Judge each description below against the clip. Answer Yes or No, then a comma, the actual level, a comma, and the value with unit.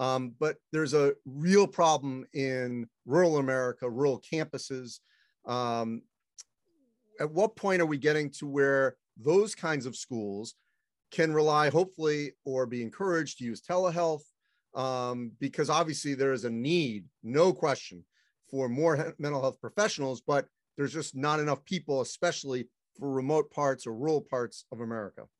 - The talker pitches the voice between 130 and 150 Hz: Yes, medium, 140 Hz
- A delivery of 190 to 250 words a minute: No, average, 150 wpm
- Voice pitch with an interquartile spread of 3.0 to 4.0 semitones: Yes, average, 3.7 semitones